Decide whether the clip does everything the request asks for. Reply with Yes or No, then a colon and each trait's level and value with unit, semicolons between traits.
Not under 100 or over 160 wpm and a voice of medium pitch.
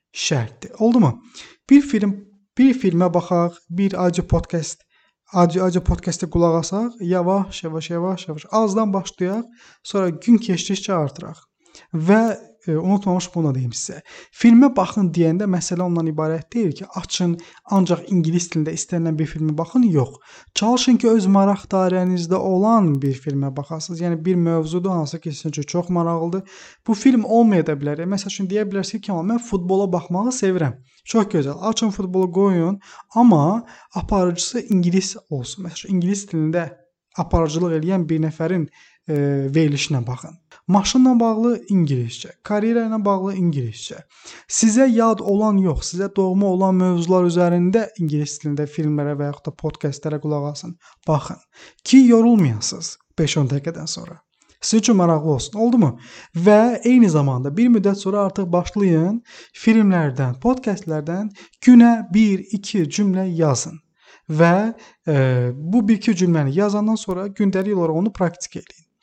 Yes: average, 140 wpm; medium, 180 Hz